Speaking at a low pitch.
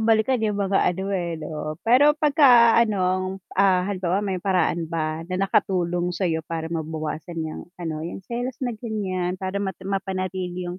No: medium, 185 Hz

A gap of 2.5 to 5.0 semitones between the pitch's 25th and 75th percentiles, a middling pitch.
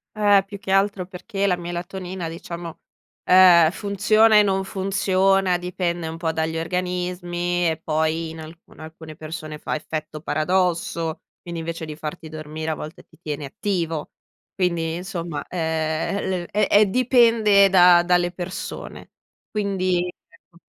Yes: average, 2.9 semitones; medium, 175 Hz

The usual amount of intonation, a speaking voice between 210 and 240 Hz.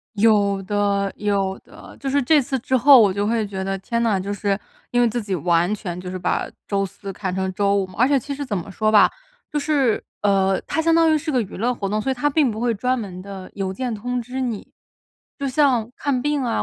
Yes: average, 4.7 semitones; high, 215 Hz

